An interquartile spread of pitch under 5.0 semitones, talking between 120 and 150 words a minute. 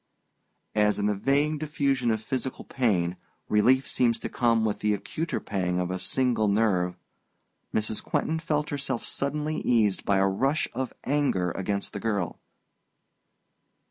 No: wide, 5.4 semitones; average, 145 wpm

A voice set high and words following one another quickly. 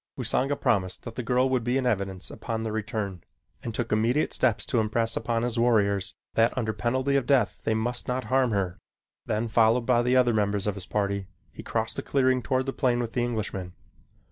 No: low, 115 Hz; fast, 210 wpm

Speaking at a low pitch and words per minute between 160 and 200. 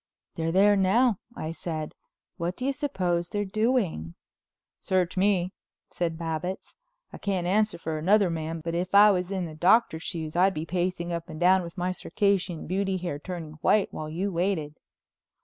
No: medium, 180 Hz; average, 175 wpm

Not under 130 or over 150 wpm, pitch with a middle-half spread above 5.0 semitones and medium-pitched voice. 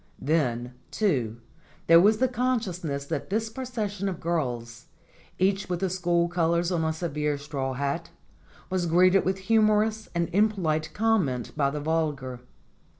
Yes: average, 145 wpm; wide, 5.4 semitones; medium, 170 Hz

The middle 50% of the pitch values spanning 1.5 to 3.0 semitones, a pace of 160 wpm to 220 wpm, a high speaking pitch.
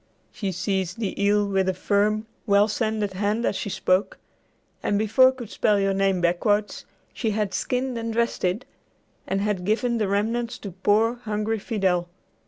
Yes: narrow, 2.4 semitones; average, 170 wpm; high, 205 Hz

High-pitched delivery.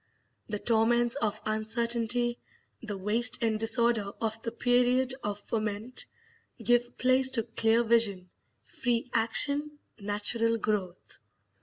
Yes: high, 230 Hz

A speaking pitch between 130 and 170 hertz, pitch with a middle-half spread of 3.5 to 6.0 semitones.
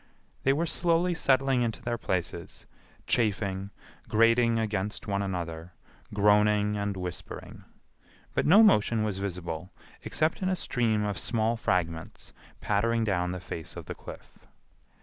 No: low, 105 Hz; average, 3.8 semitones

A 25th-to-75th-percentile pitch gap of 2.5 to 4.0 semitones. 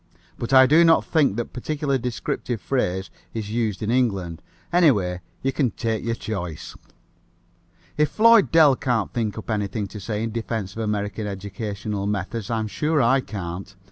No: average, 4.4 semitones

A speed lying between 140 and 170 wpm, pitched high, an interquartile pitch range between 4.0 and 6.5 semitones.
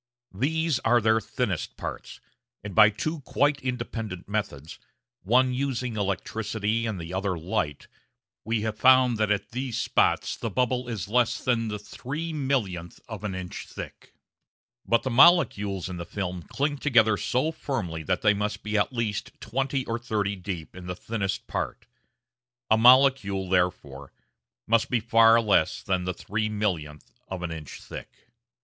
No: average, 160 wpm; low, 110 Hz; average, 4.8 semitones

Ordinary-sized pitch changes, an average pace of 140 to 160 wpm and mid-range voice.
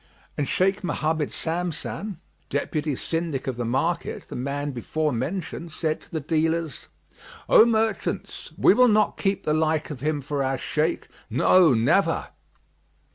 Yes: average, 3.5 semitones; average, 150 wpm; medium, 155 Hz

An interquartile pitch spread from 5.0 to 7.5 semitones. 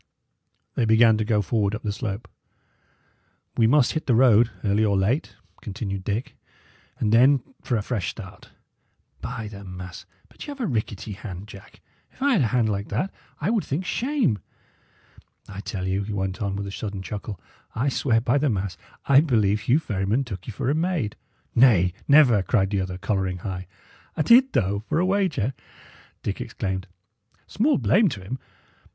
Yes: wide, 5.5 semitones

